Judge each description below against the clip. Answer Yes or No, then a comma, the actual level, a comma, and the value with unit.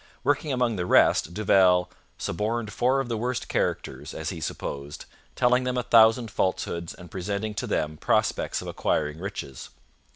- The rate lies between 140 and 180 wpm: Yes, average, 160 wpm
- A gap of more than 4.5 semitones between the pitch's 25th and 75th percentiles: Yes, wide, 5.6 semitones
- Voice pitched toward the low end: Yes, low, 105 Hz